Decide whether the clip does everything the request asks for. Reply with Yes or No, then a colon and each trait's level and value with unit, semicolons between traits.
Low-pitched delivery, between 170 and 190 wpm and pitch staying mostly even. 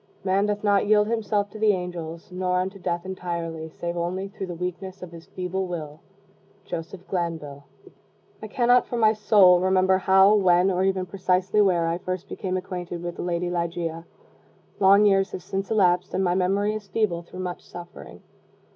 No: medium, 185 Hz; average, 180 wpm; narrow, 2.2 semitones